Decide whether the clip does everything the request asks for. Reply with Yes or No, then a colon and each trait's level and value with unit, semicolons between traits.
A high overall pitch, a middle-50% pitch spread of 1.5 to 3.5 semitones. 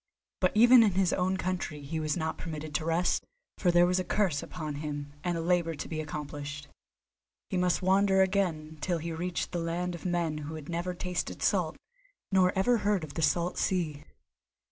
No: medium, 170 Hz; average, 2.9 semitones